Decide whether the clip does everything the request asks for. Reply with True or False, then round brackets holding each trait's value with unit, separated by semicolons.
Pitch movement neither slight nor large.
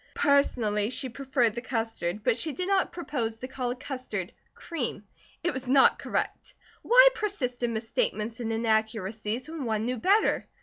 True (4.1 semitones)